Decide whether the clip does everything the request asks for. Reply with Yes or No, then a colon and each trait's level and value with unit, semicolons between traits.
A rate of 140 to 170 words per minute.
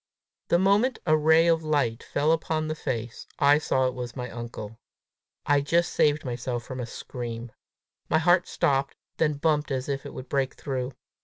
No: average, 180 wpm